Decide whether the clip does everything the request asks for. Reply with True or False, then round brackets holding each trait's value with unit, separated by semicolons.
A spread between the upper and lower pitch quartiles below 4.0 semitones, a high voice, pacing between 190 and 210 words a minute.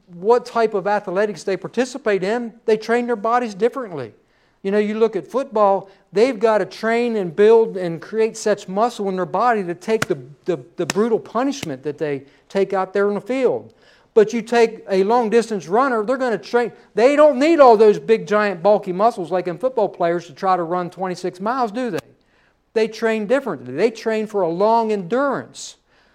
True (3.6 semitones; 215 Hz; 200 wpm)